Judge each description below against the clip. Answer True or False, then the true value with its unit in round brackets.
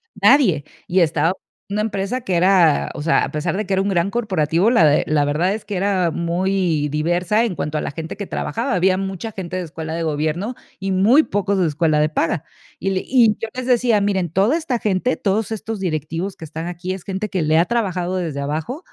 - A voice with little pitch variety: False (4.0 semitones)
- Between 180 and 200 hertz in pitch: True (185 Hz)